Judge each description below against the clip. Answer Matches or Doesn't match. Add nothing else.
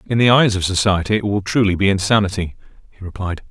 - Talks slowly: Doesn't match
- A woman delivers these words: Doesn't match